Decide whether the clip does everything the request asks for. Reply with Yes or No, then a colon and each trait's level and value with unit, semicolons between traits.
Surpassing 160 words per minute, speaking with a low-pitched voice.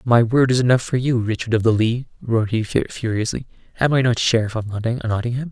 Yes: fast, 205 wpm; low, 120 Hz